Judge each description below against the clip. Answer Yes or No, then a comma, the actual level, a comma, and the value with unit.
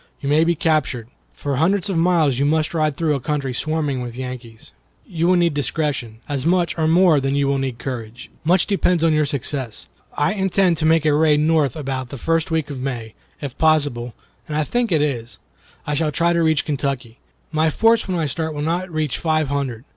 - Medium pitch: Yes, medium, 150 Hz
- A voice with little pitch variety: No, average, 3.4 semitones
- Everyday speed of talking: No, fast, 215 wpm